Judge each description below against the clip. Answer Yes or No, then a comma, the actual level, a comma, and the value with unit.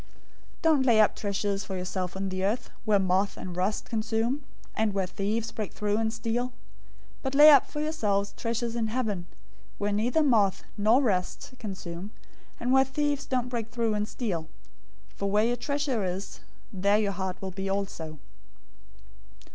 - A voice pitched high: Yes, high, 215 Hz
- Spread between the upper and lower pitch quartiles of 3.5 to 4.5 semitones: Yes, average, 3.8 semitones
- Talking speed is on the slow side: No, average, 175 wpm